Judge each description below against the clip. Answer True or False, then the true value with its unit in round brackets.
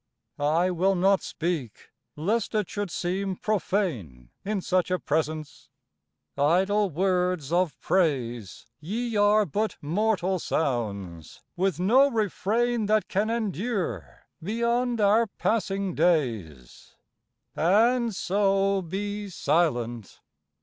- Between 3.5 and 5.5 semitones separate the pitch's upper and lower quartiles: True (5.1 semitones)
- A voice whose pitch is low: False (185 Hz)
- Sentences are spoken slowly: True (105 wpm)